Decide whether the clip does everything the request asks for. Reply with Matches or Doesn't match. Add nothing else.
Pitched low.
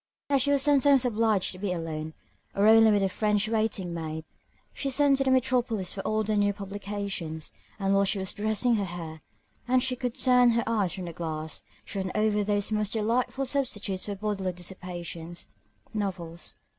Doesn't match